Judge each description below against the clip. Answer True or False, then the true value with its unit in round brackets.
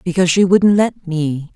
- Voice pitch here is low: False (175 Hz)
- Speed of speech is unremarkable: True (195 wpm)